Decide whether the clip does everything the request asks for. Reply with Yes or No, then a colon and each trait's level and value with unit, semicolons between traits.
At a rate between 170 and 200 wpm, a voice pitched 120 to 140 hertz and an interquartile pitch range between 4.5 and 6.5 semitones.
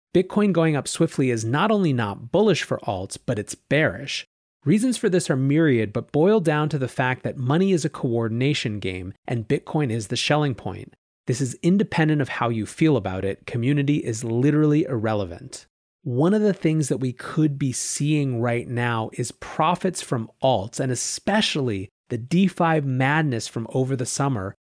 Yes: average, 180 wpm; low, 135 Hz; average, 5.1 semitones